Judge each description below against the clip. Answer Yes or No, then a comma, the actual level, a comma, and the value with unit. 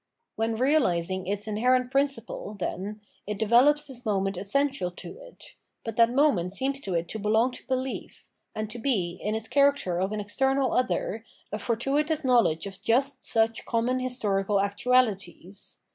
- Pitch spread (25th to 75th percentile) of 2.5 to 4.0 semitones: No, average, 4.6 semitones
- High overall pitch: Yes, high, 225 Hz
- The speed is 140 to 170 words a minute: Yes, average, 160 wpm